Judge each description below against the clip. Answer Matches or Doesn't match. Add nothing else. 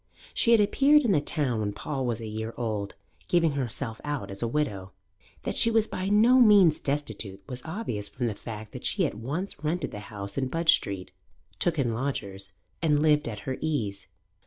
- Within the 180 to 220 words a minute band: Matches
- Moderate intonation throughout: Doesn't match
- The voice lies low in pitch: Matches